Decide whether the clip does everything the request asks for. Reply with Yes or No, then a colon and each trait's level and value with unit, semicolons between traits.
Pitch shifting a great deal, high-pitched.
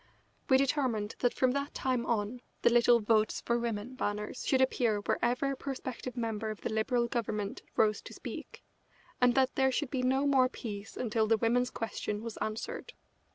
No: average, 3.0 semitones; high, 240 Hz